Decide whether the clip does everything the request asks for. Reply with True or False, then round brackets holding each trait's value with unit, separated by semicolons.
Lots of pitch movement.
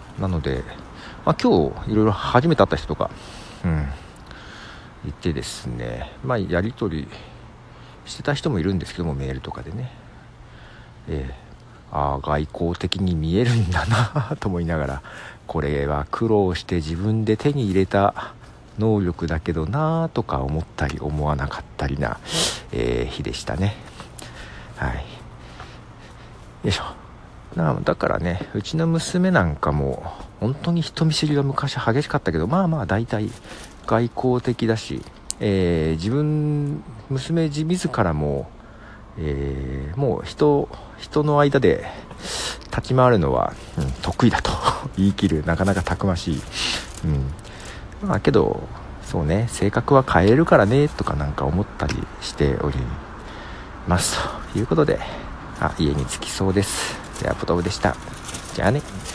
True (7.8 semitones)